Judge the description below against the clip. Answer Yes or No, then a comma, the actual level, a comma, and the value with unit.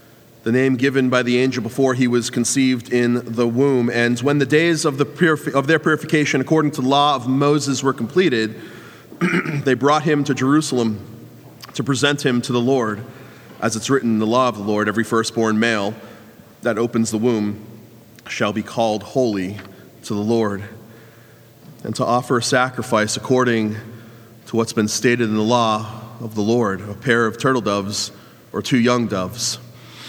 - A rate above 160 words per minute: Yes, average, 180 wpm